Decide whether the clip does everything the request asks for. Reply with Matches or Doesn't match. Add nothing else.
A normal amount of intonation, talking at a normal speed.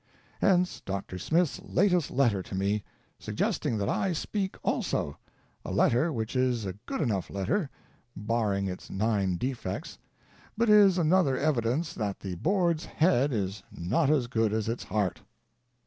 Doesn't match